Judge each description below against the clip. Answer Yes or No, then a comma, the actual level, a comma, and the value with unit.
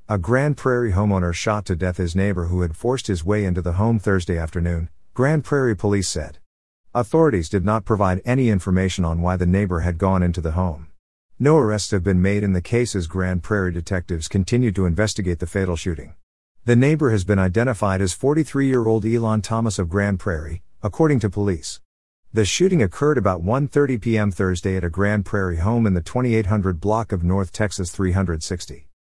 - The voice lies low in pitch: Yes, low, 100 Hz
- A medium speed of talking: Yes, average, 185 wpm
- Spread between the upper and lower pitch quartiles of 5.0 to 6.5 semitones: No, average, 3.8 semitones